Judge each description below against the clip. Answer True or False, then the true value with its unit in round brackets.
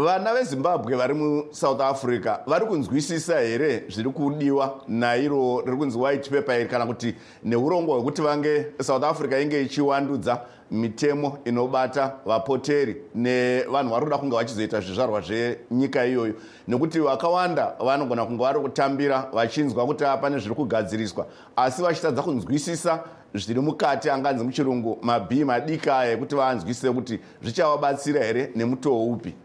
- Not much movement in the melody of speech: False (3.5 semitones)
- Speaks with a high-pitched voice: False (135 Hz)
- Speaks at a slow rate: True (130 wpm)